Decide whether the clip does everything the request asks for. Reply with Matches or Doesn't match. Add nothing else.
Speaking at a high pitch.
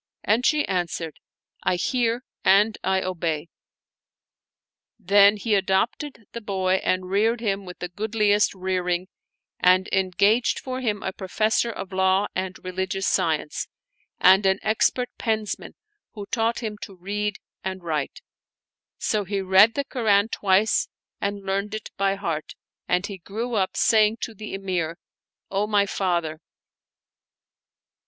Matches